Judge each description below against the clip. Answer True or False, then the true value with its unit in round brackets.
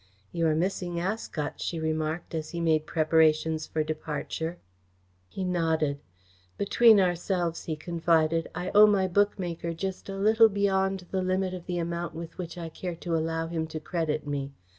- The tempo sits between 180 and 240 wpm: False (165 wpm)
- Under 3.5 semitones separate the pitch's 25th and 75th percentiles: True (2.7 semitones)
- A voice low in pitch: False (170 Hz)